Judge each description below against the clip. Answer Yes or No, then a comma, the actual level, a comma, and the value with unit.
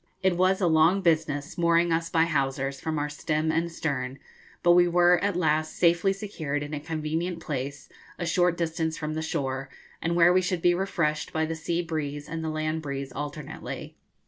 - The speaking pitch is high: No, medium, 160 Hz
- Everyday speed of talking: Yes, average, 195 wpm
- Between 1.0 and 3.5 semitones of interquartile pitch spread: Yes, narrow, 2.5 semitones